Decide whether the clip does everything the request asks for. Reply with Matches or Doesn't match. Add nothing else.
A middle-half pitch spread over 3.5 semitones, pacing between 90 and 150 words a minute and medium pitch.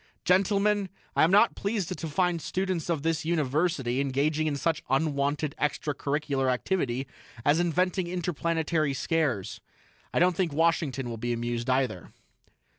Matches